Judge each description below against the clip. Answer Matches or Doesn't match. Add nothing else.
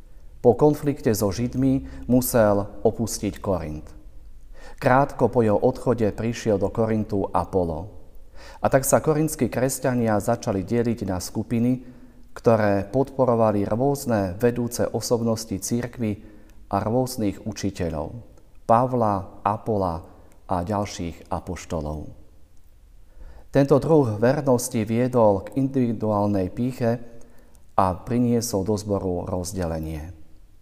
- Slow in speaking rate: Matches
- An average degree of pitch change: Matches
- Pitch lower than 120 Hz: Matches